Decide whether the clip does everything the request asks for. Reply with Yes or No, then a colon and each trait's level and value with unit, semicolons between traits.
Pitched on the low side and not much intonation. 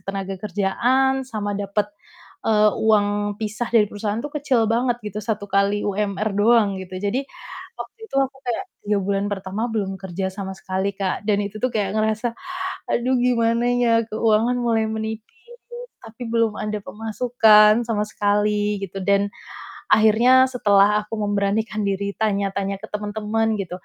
No: high, 210 Hz; narrow, 2.1 semitones